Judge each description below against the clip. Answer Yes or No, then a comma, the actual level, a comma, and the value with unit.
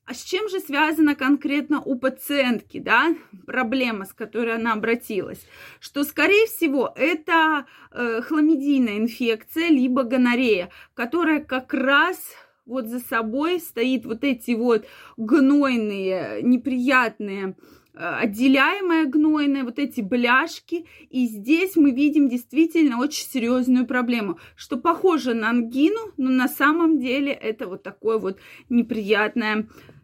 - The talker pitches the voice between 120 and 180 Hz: No, very high, 260 Hz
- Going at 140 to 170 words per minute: No, average, 125 wpm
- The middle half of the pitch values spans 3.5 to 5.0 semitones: Yes, average, 4.6 semitones